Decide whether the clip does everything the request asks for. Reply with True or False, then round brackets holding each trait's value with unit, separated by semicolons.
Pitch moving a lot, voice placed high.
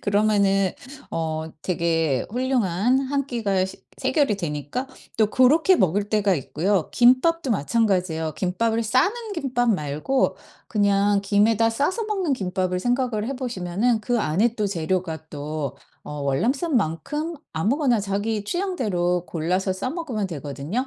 True (6.1 semitones; 205 Hz)